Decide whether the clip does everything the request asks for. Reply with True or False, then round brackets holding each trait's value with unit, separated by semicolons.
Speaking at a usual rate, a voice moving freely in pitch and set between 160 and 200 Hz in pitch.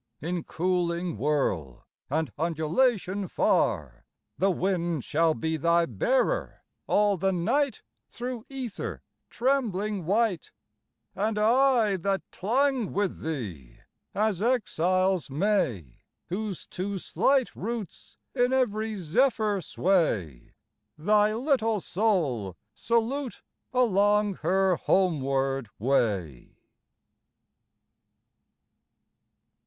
False (90 wpm; 5.7 semitones; 190 Hz)